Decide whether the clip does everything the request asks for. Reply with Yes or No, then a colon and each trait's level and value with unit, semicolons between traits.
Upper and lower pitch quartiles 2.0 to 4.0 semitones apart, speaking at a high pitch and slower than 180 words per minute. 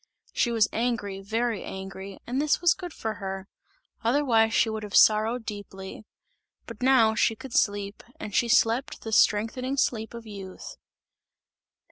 Yes: average, 2.9 semitones; high, 220 Hz; average, 150 wpm